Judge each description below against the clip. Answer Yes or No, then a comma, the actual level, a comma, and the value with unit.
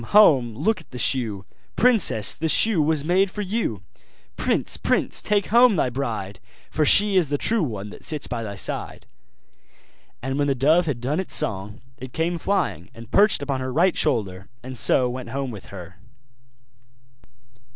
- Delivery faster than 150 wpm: Yes, average, 175 wpm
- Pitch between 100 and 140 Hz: Yes, low, 135 Hz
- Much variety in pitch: Yes, wide, 7.4 semitones